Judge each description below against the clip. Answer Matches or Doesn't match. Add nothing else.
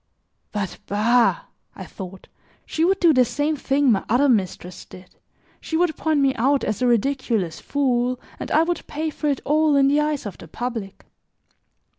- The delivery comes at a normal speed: Matches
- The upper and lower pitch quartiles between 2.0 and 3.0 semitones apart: Doesn't match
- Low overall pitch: Doesn't match